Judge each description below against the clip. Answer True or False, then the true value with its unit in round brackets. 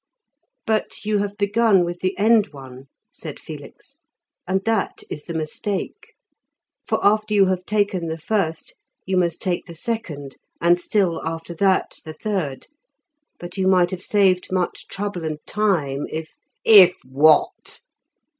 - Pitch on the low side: False (185 Hz)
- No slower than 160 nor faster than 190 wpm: False (150 wpm)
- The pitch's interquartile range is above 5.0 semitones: False (4.0 semitones)